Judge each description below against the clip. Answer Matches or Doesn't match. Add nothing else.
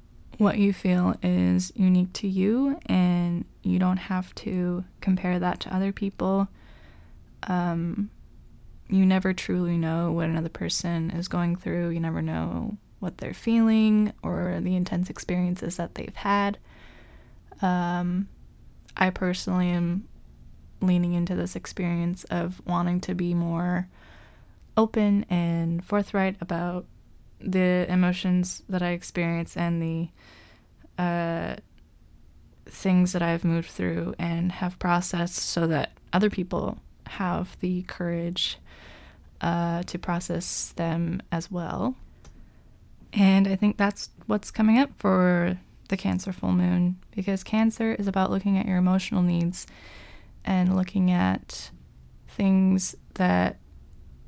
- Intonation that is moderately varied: Doesn't match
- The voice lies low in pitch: Doesn't match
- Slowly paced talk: Matches